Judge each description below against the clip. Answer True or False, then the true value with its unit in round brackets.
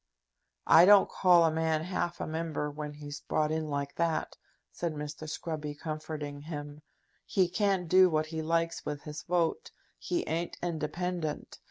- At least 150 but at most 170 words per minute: True (160 wpm)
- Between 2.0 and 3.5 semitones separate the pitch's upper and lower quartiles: True (2.4 semitones)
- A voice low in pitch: False (160 Hz)